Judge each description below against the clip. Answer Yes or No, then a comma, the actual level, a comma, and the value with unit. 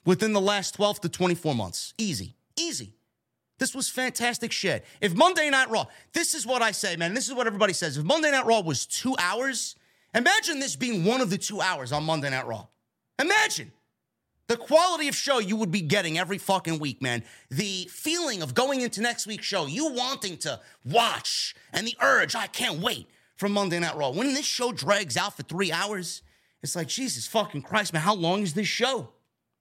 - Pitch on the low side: No, high, 205 Hz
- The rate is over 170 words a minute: Yes, fast, 205 wpm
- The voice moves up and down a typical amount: No, wide, 7.0 semitones